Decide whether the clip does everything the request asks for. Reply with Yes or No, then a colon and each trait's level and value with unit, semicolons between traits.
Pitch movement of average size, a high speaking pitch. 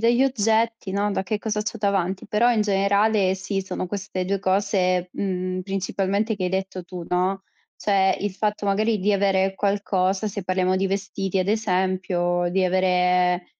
No: narrow, 1.8 semitones; high, 195 Hz